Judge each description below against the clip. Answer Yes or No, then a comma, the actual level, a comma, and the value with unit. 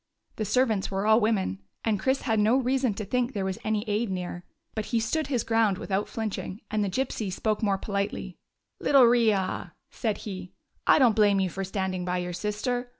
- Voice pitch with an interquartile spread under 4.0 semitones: Yes, average, 3.2 semitones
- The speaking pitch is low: No, high, 210 Hz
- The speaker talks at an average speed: No, fast, 210 wpm